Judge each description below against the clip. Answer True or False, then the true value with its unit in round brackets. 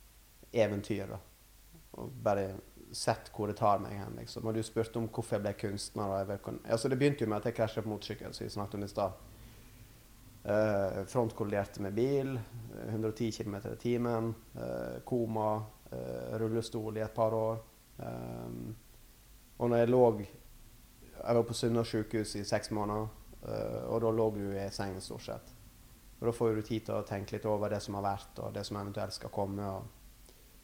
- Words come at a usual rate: True (175 wpm)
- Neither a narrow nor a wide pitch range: False (2.2 semitones)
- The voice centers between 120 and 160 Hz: False (110 Hz)